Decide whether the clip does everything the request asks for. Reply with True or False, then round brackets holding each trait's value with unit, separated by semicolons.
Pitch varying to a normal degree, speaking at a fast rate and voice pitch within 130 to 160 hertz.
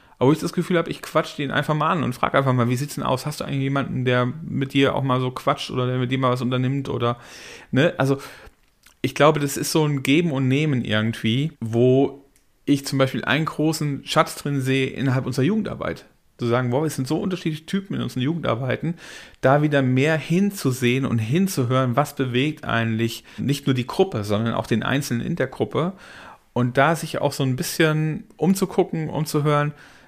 True (3.4 semitones; 205 wpm; 140 Hz)